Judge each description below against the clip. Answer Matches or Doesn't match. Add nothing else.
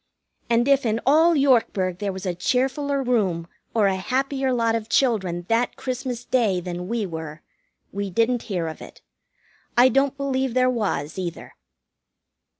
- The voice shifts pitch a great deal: Matches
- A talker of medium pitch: Doesn't match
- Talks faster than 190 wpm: Doesn't match